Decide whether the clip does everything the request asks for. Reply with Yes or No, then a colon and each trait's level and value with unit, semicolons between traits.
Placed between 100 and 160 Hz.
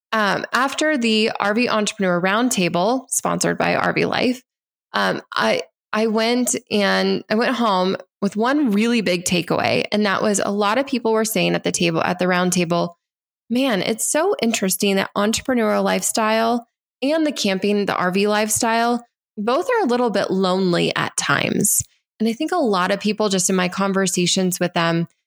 No: high, 210 Hz